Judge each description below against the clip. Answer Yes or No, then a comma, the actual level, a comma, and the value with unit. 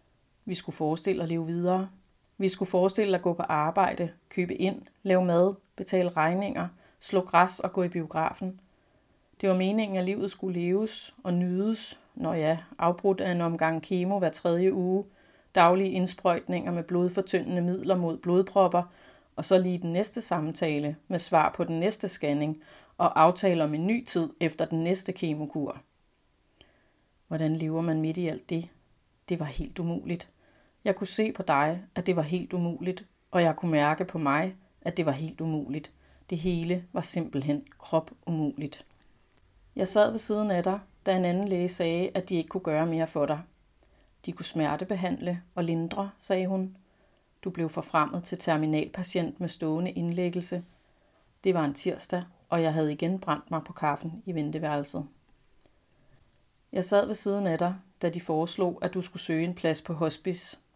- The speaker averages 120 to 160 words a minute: No, average, 175 wpm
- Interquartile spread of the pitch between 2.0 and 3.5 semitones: Yes, average, 2.7 semitones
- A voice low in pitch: No, medium, 175 Hz